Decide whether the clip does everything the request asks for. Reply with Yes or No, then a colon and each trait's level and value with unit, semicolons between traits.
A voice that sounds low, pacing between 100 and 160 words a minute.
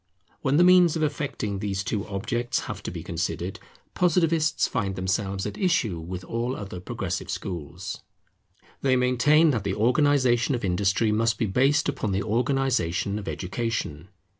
Yes: low, 115 Hz; average, 155 wpm